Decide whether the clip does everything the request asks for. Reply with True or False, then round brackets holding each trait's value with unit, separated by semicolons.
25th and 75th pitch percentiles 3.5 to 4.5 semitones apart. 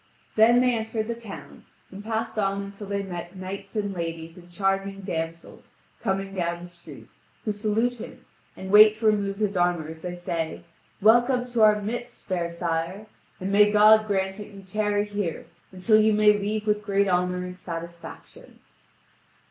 False (2.9 semitones)